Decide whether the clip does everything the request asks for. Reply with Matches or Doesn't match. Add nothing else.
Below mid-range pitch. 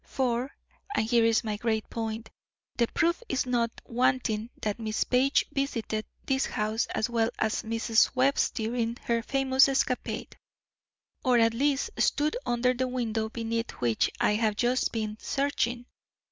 Doesn't match